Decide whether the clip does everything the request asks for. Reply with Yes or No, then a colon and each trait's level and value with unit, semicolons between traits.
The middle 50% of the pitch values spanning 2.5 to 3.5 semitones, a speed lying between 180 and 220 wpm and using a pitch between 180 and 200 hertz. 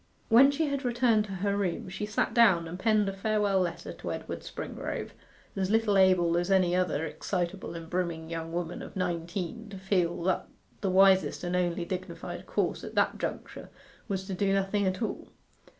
Yes: average, 2.8 semitones; average, 185 wpm; high, 190 Hz